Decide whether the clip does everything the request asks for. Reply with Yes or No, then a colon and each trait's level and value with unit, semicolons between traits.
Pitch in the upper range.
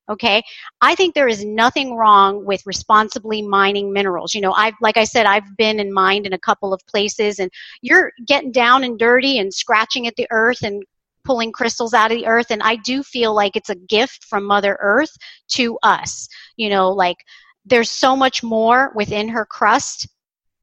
Yes: high, 220 Hz